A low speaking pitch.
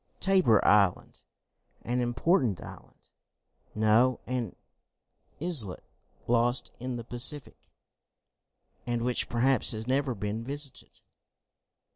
Yes: low, 120 Hz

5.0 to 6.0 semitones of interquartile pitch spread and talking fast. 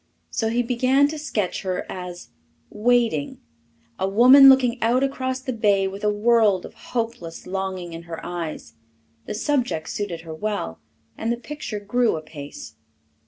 No: wide, 5.4 semitones; average, 155 wpm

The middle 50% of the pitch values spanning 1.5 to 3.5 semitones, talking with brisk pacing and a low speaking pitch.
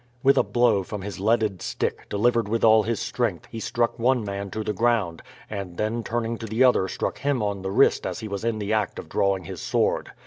Yes: average, 2.8 semitones; fast, 235 wpm; low, 110 Hz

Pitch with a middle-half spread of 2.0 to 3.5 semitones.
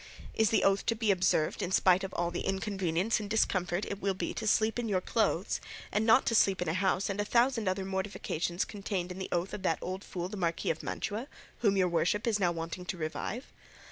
Yes: average, 2.8 semitones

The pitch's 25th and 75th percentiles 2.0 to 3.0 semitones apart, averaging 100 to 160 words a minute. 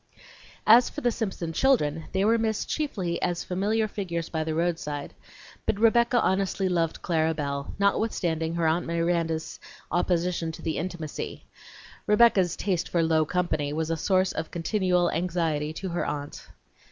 No: average, 3.5 semitones; average, 155 wpm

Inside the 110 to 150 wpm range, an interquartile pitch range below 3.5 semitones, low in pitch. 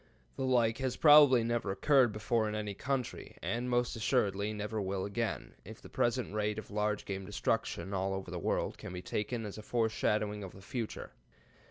No: average, 190 wpm; average, 3.0 semitones; low, 110 Hz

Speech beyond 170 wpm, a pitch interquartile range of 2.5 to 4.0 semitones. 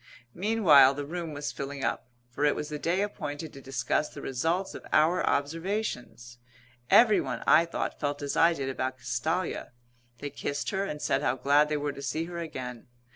Yes: average, 185 wpm; average, 3.6 semitones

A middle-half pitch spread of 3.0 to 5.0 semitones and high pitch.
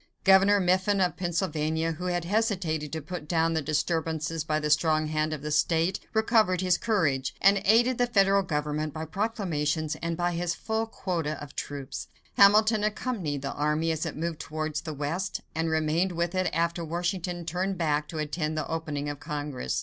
No: average, 3.5 semitones; medium, 165 Hz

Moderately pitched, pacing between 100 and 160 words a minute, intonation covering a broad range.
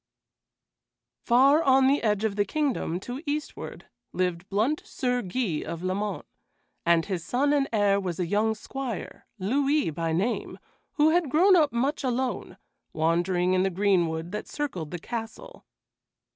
No: high, 215 Hz; average, 150 wpm; wide, 7.0 semitones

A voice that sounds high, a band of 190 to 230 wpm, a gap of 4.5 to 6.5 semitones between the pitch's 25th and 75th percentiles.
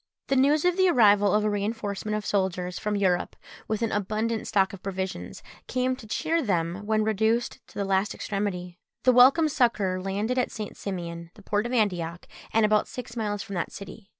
No: high, 210 Hz; average, 195 wpm; average, 3.2 semitones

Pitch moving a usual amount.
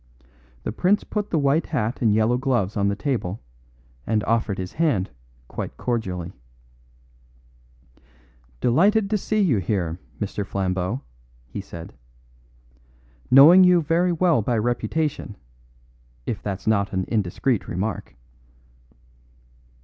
No: wide, 7.5 semitones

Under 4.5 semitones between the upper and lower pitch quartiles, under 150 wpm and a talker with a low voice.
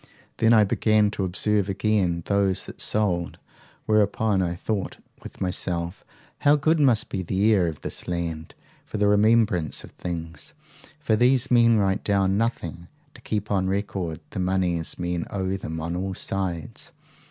No: average, 3.5 semitones; average, 160 wpm; very low, 95 Hz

